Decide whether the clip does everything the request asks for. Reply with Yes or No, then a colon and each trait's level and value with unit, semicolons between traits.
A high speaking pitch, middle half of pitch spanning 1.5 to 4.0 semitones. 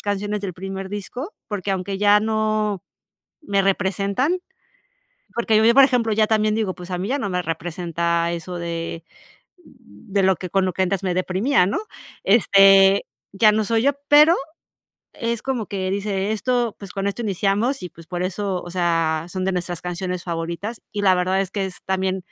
Yes: high, 195 Hz; average, 2.9 semitones